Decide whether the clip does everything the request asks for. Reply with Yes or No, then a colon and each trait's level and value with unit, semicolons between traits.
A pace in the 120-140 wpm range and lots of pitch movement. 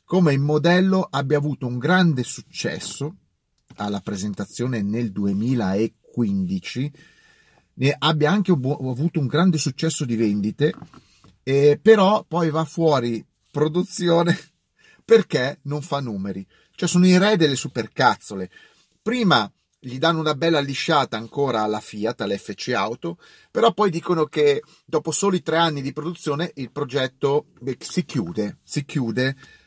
Yes: average, 135 wpm; wide, 5.7 semitones